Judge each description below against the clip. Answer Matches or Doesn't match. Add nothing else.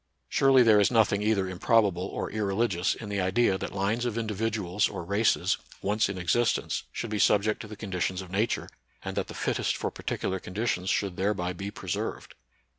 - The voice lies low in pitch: Matches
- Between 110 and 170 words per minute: Doesn't match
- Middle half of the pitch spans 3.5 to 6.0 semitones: Doesn't match